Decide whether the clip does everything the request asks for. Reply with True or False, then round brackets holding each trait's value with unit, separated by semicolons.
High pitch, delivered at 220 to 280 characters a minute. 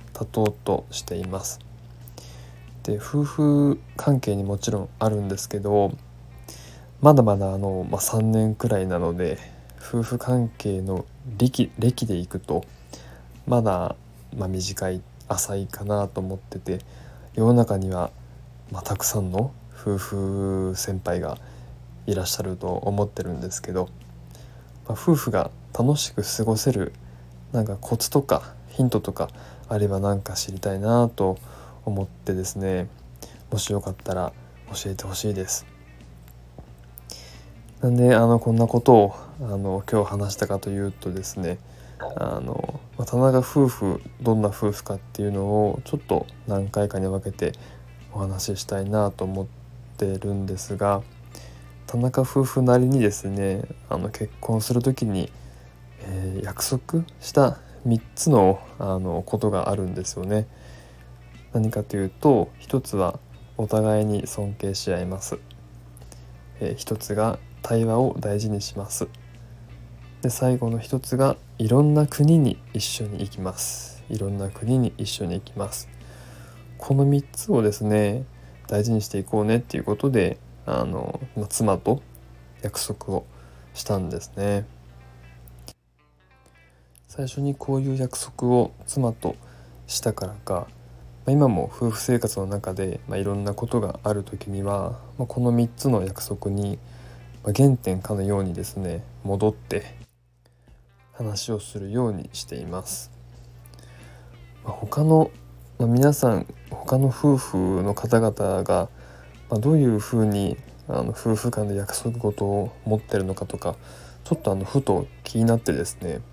False (100 Hz; 260 characters per minute)